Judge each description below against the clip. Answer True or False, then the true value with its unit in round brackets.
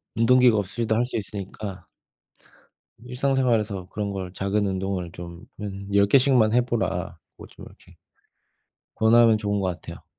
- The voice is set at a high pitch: False (105 Hz)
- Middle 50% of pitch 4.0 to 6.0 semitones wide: False (3.5 semitones)